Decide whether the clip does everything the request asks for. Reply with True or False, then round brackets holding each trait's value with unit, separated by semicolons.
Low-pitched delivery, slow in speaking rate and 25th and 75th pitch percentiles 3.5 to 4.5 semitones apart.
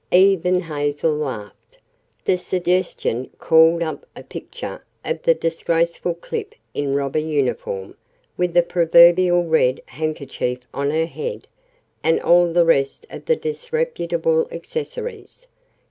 False (170 Hz; 120 wpm; 4.0 semitones)